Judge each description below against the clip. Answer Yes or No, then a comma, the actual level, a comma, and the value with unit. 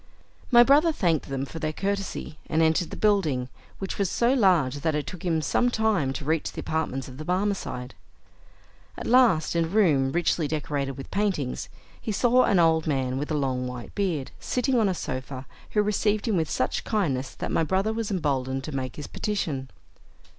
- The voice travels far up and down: Yes, wide, 6.8 semitones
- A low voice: No, medium, 160 Hz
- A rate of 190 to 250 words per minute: Yes, average, 195 wpm